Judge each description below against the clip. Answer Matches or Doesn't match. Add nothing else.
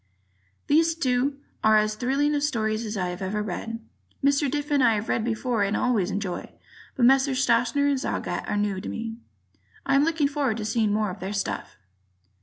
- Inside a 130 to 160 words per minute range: Doesn't match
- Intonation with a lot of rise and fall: Doesn't match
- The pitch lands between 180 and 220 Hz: Doesn't match